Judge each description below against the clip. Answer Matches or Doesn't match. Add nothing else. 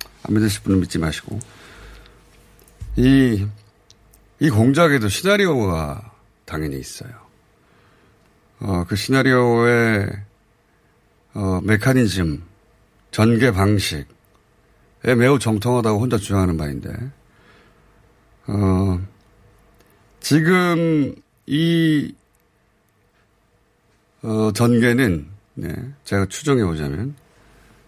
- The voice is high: Doesn't match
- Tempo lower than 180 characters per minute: Matches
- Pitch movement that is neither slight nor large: Matches